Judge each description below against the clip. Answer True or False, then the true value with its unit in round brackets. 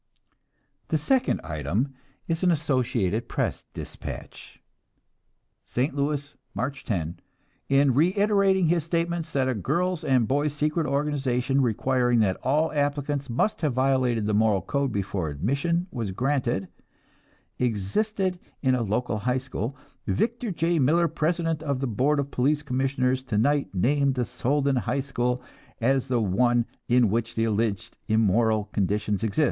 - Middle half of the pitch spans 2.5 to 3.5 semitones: False (4.6 semitones)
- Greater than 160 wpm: False (145 wpm)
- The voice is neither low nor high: False (130 Hz)